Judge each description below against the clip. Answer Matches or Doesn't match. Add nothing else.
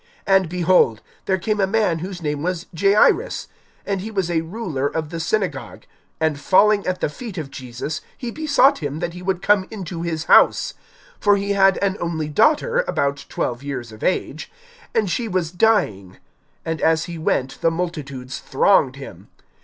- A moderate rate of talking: Matches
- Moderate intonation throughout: Matches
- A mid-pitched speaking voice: Matches